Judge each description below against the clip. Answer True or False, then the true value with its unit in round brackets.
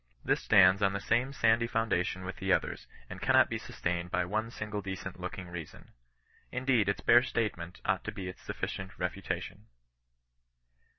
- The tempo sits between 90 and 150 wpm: False (165 wpm)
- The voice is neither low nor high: False (95 Hz)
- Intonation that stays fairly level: False (3.7 semitones)